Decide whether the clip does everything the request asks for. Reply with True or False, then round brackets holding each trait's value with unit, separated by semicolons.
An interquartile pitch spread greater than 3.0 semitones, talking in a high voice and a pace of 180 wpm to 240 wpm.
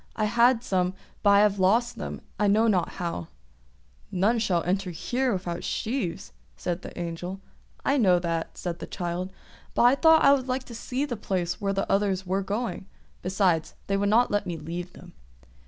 True (4.5 semitones; 195 Hz; 190 wpm)